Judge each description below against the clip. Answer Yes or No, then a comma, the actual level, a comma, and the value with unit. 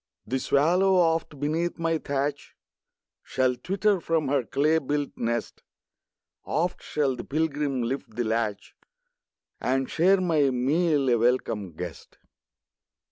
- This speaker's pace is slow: Yes, slow, 125 wpm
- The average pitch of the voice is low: No, medium, 145 Hz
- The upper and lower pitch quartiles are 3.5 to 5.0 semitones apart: Yes, average, 4.4 semitones